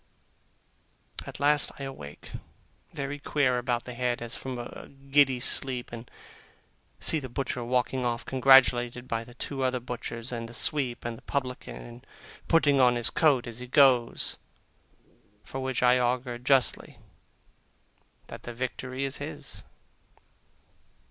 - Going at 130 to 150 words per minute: Yes, average, 140 wpm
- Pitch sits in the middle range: No, low, 125 Hz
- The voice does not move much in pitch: Yes, narrow, 1.9 semitones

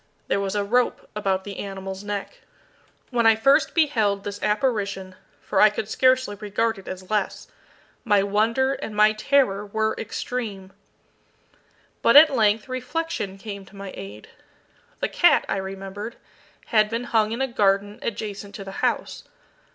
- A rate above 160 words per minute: No, average, 155 wpm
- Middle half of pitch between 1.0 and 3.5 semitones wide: Yes, average, 2.7 semitones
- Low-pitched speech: No, high, 210 Hz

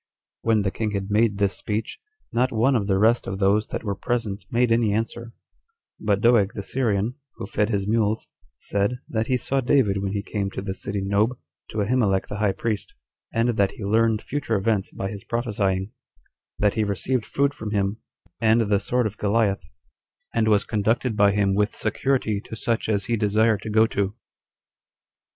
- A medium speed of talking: Yes, average, 190 wpm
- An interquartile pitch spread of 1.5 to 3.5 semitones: Yes, narrow, 2.4 semitones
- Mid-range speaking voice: No, low, 105 Hz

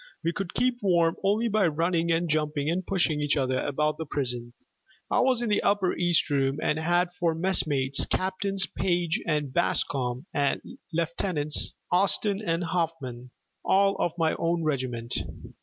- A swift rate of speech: No, average, 155 wpm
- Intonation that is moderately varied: Yes, average, 4.2 semitones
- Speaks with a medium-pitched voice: Yes, medium, 165 Hz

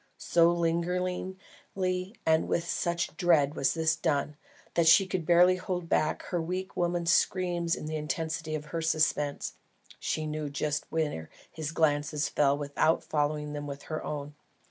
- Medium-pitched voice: Yes, medium, 160 Hz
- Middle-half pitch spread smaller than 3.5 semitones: Yes, narrow, 2.6 semitones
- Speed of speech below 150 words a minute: No, average, 155 wpm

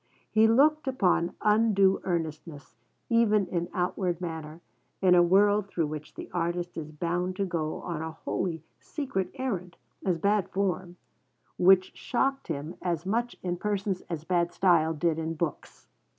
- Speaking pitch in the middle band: Yes, medium, 180 Hz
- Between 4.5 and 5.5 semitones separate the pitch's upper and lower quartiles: No, average, 3.3 semitones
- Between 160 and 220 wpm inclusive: No, average, 150 wpm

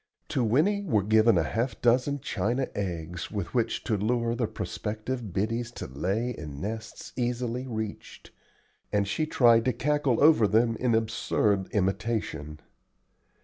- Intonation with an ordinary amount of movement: Yes, average, 3.3 semitones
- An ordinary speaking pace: Yes, average, 145 wpm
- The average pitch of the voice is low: Yes, low, 115 Hz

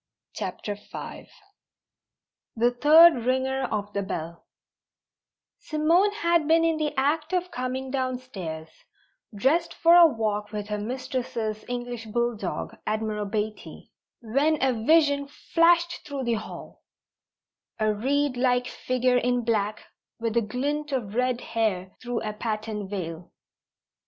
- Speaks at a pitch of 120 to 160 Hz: No, high, 245 Hz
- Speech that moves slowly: Yes, slow, 125 wpm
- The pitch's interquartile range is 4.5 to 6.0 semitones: Yes, average, 5.0 semitones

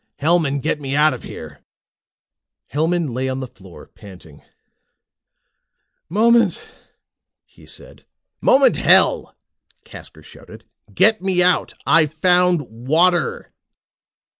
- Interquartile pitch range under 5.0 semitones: No, average, 5.3 semitones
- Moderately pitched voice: Yes, medium, 155 Hz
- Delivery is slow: Yes, slow, 105 wpm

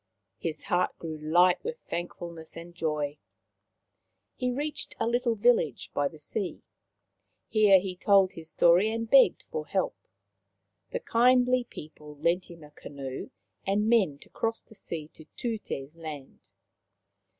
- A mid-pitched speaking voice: Yes, medium, 180 Hz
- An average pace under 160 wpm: Yes, average, 140 wpm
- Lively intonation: Yes, wide, 6.5 semitones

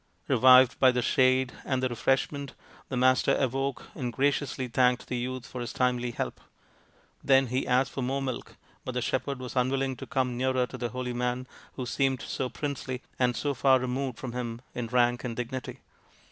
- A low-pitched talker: Yes, low, 130 Hz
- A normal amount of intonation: No, narrow, 1.2 semitones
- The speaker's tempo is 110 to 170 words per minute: No, average, 190 wpm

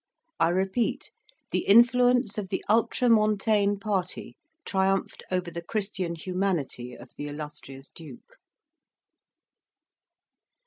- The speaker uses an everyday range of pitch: Yes, average, 4.3 semitones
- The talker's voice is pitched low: No, high, 190 Hz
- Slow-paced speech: Yes, slow, 100 wpm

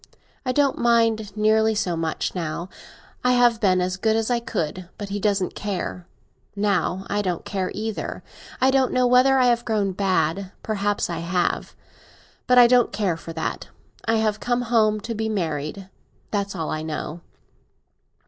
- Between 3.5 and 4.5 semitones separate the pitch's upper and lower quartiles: Yes, average, 3.8 semitones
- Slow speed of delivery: No, average, 165 wpm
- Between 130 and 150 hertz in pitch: No, high, 205 Hz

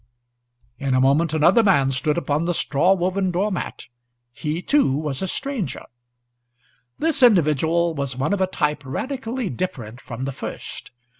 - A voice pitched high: No, medium, 165 Hz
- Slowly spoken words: No, average, 155 wpm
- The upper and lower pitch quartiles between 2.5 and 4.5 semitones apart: No, wide, 5.6 semitones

